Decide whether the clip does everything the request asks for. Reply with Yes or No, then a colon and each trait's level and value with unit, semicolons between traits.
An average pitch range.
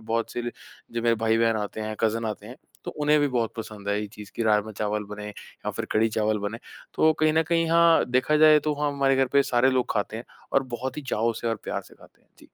Yes: average, 4.4 semitones